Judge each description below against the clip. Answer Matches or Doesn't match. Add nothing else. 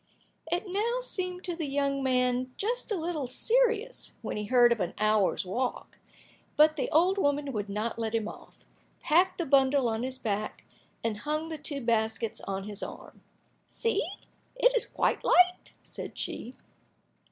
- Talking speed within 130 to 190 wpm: Matches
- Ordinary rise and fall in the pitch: Doesn't match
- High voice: Matches